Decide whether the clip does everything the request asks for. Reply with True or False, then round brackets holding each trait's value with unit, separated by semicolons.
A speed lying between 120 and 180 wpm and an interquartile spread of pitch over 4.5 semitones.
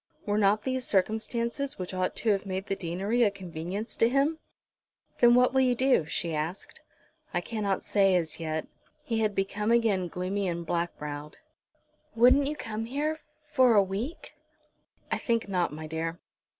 True (170 wpm; 5.0 semitones)